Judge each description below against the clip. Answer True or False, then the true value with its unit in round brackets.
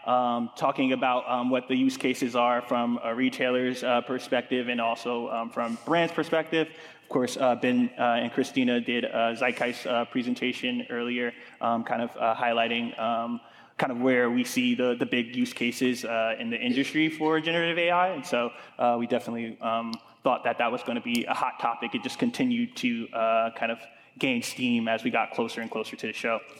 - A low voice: True (125 Hz)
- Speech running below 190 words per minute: False (200 wpm)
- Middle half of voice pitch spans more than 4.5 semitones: True (5.0 semitones)